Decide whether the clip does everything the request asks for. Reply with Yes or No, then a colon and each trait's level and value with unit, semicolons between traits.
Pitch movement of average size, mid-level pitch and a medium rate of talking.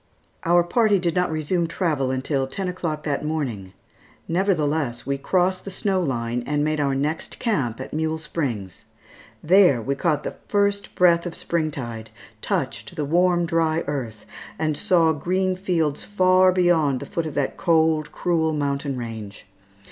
Yes: average, 4.3 semitones; medium, 160 Hz; average, 160 wpm